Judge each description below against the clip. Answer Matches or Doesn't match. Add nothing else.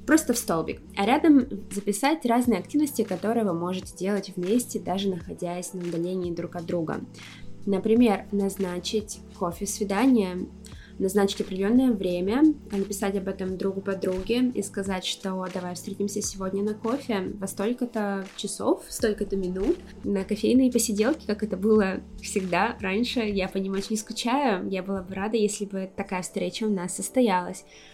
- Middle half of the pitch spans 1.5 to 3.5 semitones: Matches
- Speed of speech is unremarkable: Matches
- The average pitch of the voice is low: Doesn't match